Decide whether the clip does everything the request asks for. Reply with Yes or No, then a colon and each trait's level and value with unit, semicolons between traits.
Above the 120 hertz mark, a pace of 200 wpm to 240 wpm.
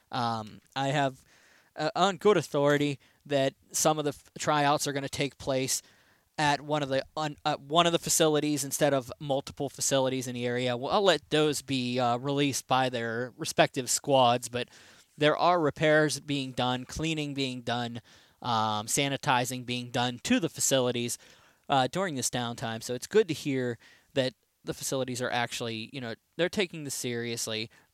No: low, 135 Hz; average, 175 wpm